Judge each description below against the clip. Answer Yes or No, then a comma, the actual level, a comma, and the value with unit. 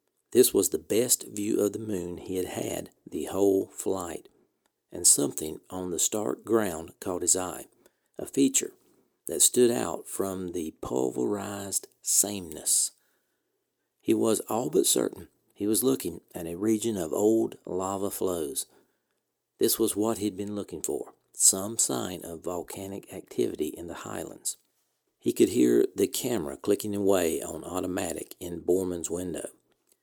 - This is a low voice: Yes, low, 100 Hz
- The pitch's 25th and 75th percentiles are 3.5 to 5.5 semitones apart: No, average, 3.1 semitones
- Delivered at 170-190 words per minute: No, average, 150 wpm